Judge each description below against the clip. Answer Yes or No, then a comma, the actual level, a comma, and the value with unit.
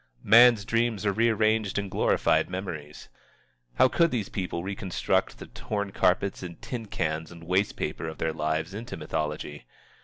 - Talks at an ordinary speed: Yes, average, 155 wpm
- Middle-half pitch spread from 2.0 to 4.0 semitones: No, average, 5.2 semitones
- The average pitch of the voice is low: Yes, very low, 95 Hz